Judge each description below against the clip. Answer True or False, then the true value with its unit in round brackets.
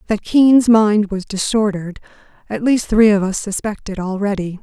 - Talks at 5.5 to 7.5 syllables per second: False (5.0 syllables/s)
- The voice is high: True (205 Hz)